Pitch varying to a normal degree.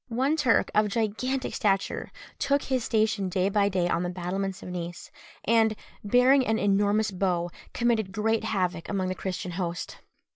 Yes: average, 3.5 semitones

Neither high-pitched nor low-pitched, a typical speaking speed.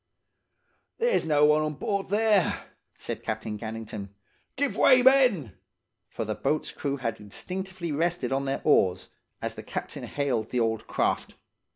Yes: medium, 150 Hz; average, 150 wpm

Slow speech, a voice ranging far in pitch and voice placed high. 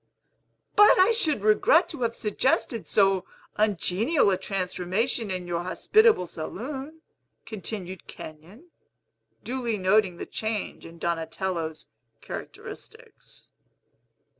Yes: slow, 100 wpm; wide, 5.9 semitones; high, 210 Hz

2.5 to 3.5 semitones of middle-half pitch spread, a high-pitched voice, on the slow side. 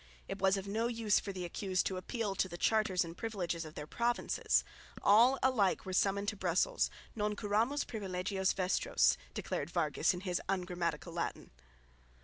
No: average, 3.0 semitones; high, 195 Hz; average, 165 wpm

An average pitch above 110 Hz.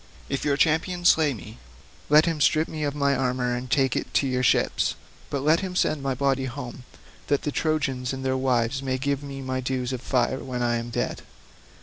Yes: low, 135 Hz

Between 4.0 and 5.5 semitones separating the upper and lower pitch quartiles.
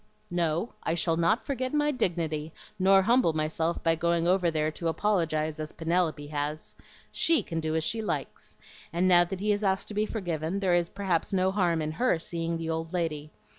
No: average, 3.1 semitones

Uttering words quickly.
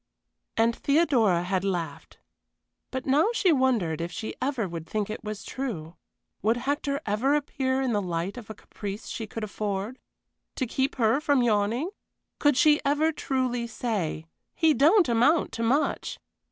No: average, 160 wpm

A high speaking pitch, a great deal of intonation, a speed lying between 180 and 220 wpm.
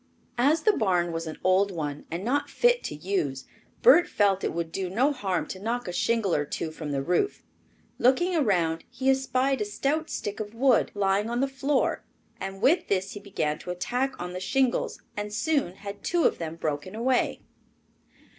Yes: high, 205 Hz; wide, 6.8 semitones; average, 195 wpm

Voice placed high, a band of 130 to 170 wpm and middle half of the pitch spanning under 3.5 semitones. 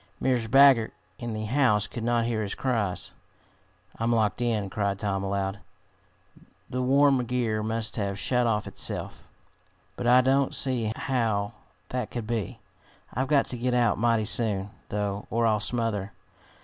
No: low, 115 Hz; average, 155 wpm; average, 3.0 semitones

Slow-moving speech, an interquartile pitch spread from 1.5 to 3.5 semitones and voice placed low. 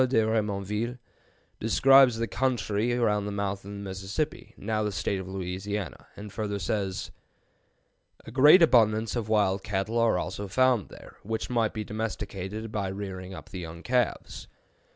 No: average, 155 wpm; average, 2.8 semitones; low, 105 Hz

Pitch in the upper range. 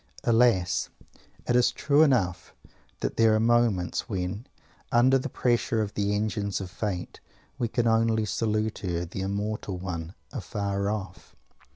No: low, 105 Hz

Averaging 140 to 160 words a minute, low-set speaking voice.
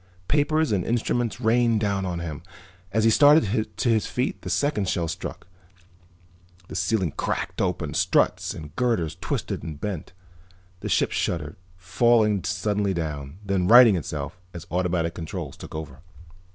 Yes: average, 150 wpm; low, 100 Hz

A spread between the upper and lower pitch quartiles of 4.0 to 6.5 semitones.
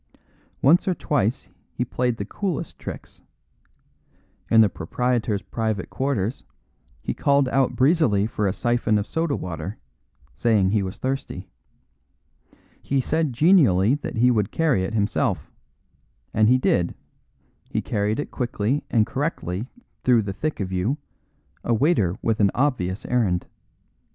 Yes: average, 5.2 semitones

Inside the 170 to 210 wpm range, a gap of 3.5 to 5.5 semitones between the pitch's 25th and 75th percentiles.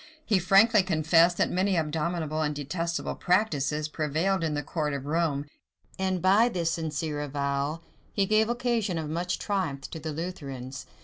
No: average, 160 wpm; average, 3.9 semitones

